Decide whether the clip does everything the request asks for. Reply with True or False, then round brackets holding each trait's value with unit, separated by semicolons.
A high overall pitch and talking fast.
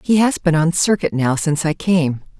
False (165 Hz; 225 wpm)